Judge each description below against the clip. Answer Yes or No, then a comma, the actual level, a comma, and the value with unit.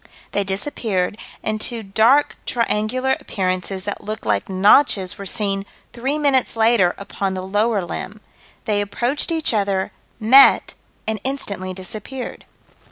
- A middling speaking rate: No, slow, 130 wpm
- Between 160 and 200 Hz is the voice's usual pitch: No, high, 210 Hz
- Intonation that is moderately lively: Yes, average, 3.8 semitones